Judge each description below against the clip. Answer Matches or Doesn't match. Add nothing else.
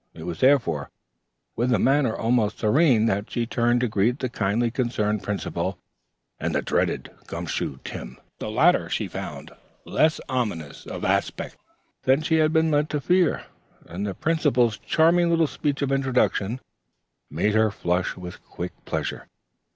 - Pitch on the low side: Matches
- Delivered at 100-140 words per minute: Doesn't match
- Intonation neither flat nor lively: Doesn't match